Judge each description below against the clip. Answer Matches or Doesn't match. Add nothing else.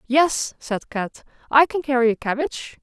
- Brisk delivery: Doesn't match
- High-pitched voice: Matches